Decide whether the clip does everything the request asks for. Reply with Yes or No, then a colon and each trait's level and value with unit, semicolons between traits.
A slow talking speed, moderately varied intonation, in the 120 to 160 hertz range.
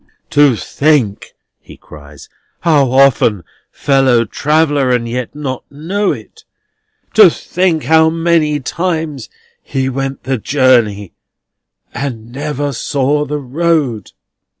Yes: slow, 110 wpm; average, 3.8 semitones; medium, 140 Hz